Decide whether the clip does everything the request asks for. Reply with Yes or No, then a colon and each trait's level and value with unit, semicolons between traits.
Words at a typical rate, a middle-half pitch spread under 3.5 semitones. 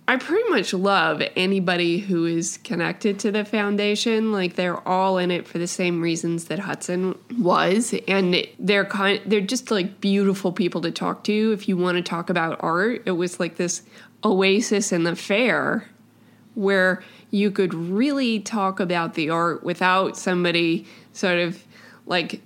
Yes: average, 165 wpm; average, 2.8 semitones